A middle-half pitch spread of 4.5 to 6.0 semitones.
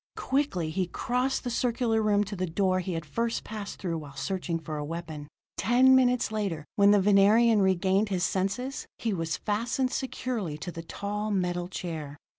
Yes: average, 4.9 semitones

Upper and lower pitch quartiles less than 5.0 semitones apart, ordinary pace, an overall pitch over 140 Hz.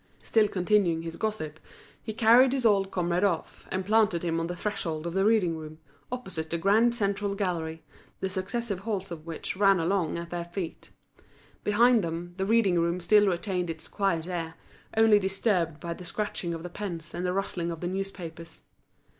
Yes: average, 3.4 semitones; average, 185 wpm; medium, 185 Hz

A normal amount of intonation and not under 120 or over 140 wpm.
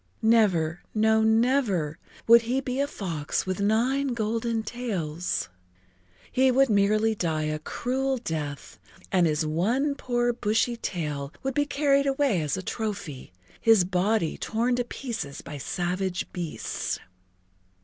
No: wide, 6.3 semitones; slow, 135 wpm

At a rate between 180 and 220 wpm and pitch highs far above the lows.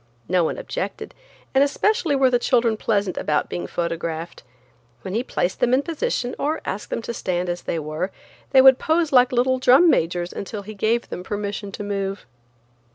Yes: average, 185 wpm; wide, 6.3 semitones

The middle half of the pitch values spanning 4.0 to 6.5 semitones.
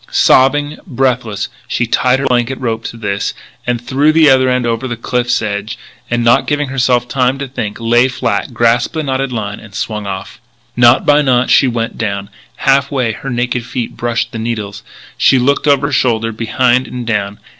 No: narrow, 2.6 semitones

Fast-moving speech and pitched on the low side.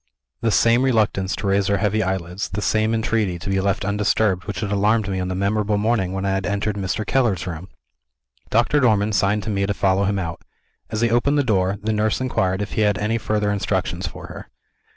Yes: fast, 220 wpm; low, 100 Hz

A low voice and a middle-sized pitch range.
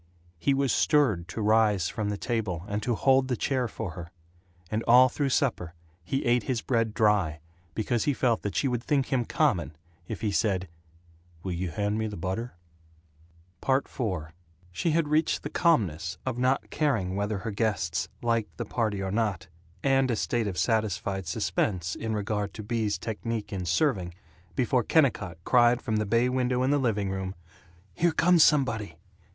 Yes: low, 110 Hz; average, 4.7 semitones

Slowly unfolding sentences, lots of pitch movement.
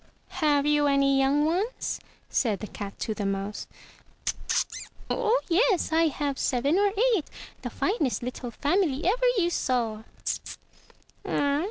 Yes: slow, 130 wpm; wide, 6.2 semitones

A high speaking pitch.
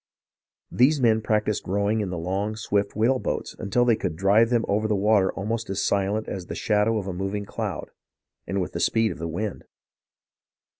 No: low, 105 Hz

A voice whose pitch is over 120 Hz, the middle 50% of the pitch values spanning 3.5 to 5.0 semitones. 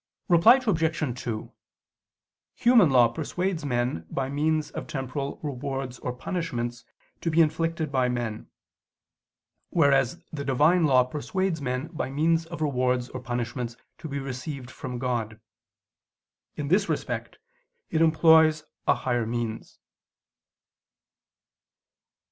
Yes: medium, 140 Hz; average, 4.4 semitones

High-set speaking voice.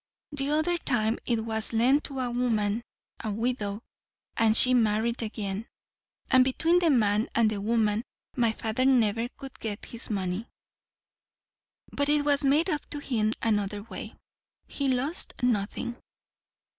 Yes: high, 235 Hz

